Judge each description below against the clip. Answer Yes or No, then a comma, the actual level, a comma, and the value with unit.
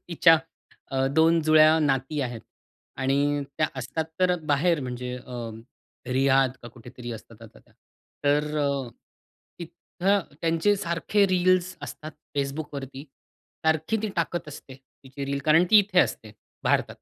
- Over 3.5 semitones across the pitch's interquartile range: Yes, average, 3.9 semitones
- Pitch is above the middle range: No, medium, 150 Hz